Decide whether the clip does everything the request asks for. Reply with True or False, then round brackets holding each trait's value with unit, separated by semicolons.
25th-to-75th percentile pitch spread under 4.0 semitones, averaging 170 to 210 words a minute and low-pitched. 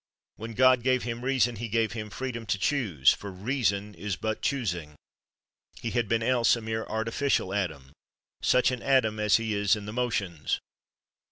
True (3.2 semitones; 175 wpm; 110 Hz)